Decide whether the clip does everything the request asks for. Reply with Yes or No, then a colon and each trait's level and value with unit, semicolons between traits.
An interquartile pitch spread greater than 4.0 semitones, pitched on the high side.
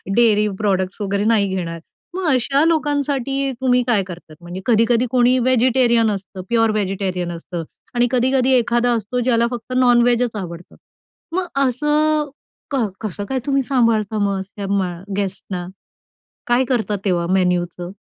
Yes: average, 4.7 semitones; high, 230 Hz